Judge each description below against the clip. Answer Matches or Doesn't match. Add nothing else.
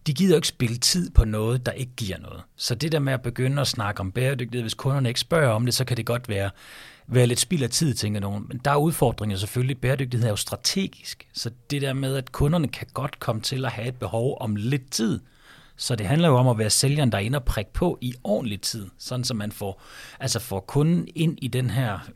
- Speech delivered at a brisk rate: Matches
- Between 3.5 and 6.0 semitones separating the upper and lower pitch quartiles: Matches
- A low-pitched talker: Matches